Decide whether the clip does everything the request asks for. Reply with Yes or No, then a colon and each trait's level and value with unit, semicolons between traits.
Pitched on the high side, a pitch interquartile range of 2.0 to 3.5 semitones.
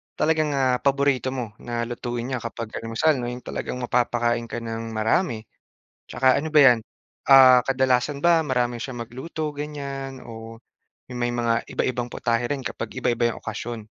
No: low, 125 Hz; narrow, 2.5 semitones